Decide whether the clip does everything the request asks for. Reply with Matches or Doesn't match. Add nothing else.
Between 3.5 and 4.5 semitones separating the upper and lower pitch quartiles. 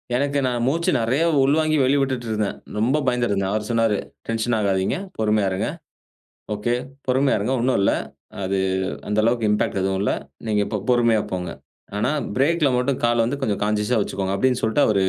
Matches